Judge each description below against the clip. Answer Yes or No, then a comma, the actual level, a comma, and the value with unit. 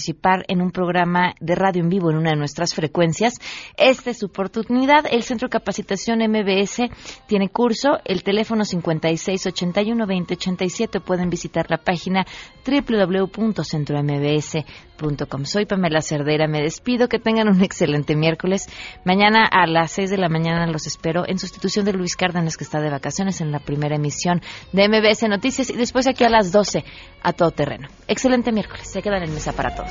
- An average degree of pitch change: Yes, average, 4.5 semitones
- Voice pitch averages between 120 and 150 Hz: No, medium, 185 Hz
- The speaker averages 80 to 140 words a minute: No, average, 175 wpm